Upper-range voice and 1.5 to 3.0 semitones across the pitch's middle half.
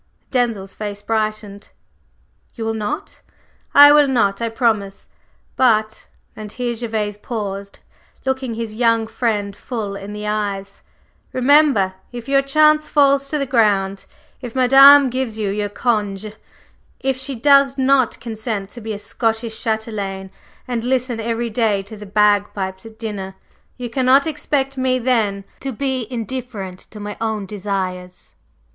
No: high, 225 Hz; average, 3.8 semitones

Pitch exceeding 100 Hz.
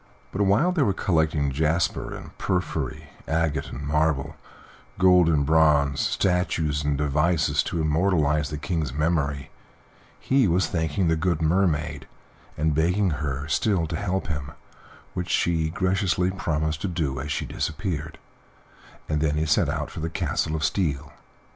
No: very low, 80 Hz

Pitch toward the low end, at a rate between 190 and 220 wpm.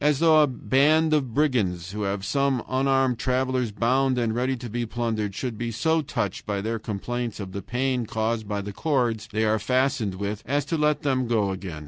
Yes: low, 120 Hz; fast, 205 wpm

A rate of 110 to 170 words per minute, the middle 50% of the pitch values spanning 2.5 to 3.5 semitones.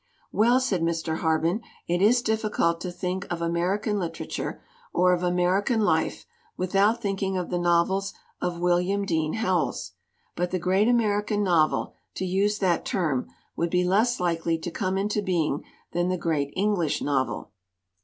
Yes: average, 155 wpm; average, 3.2 semitones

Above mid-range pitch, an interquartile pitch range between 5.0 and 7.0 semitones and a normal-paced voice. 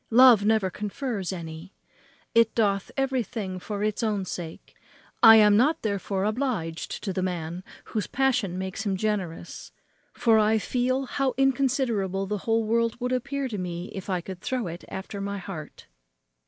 No: high, 210 Hz; average, 4.1 semitones; average, 160 wpm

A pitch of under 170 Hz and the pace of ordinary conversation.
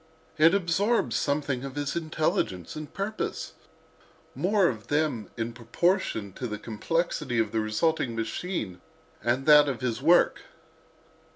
No: medium, 140 Hz; slow, 125 wpm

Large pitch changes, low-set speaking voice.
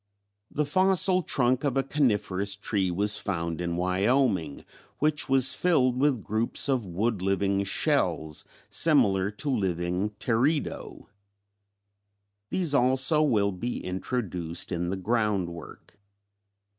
Yes: wide, 6.3 semitones; low, 105 Hz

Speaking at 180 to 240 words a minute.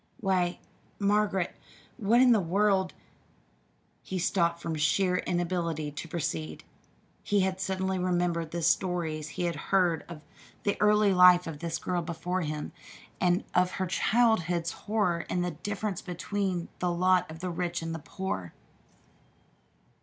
No: average, 145 wpm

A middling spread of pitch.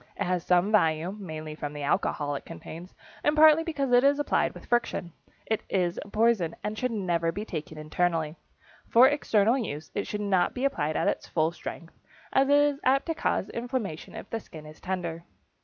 No: wide, 7.2 semitones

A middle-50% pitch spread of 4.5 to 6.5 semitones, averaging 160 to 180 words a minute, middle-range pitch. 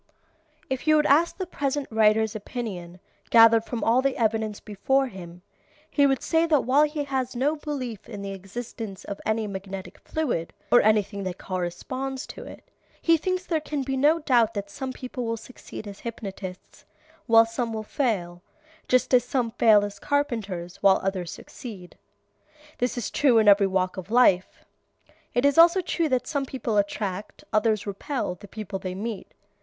No: average, 5.1 semitones; average, 175 wpm; high, 225 Hz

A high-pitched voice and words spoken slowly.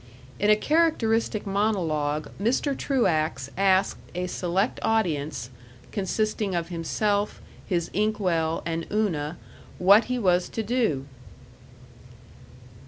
Yes: high, 195 Hz; slow, 105 wpm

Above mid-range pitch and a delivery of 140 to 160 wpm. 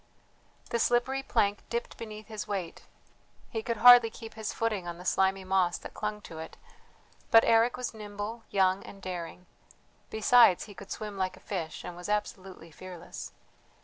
No: high, 205 Hz; average, 170 wpm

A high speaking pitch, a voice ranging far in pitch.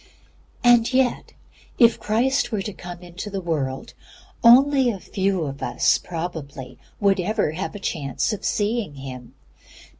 Yes: high, 195 Hz; wide, 6.5 semitones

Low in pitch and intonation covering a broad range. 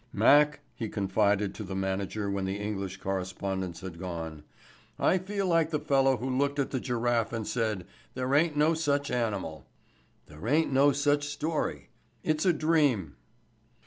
Yes: low, 120 Hz; wide, 7.1 semitones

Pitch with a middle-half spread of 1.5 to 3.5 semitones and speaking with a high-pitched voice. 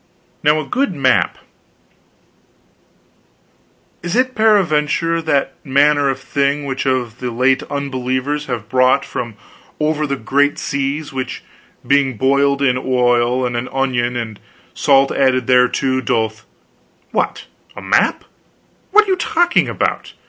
No: average, 2.7 semitones; low, 135 Hz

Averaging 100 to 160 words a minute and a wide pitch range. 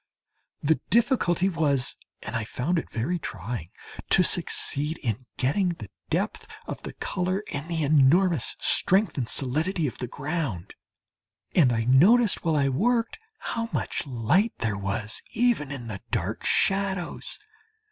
Yes: average, 145 wpm; wide, 7.0 semitones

